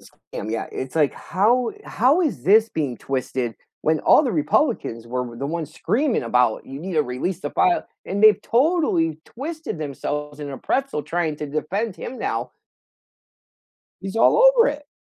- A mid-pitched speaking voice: Yes, medium, 170 Hz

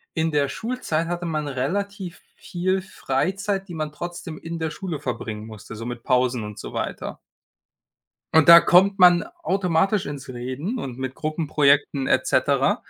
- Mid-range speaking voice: Yes, medium, 160 Hz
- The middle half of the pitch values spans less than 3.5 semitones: No, wide, 5.5 semitones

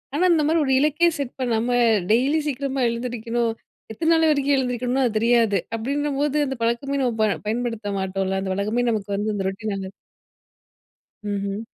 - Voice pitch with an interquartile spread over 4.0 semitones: Yes, average, 4.5 semitones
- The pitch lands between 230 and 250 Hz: Yes, high, 240 Hz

